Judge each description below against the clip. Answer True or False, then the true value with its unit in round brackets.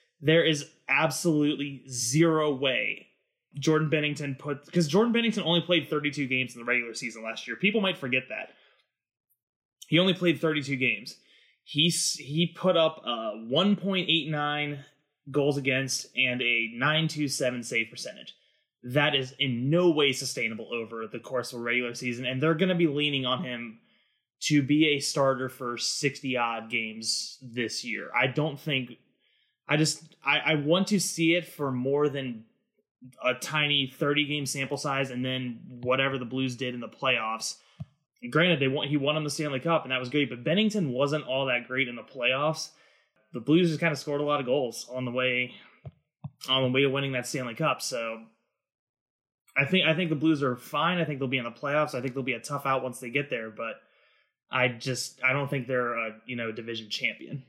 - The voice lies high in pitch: False (140 Hz)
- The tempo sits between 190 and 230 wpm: True (200 wpm)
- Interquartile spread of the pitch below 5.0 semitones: True (3.8 semitones)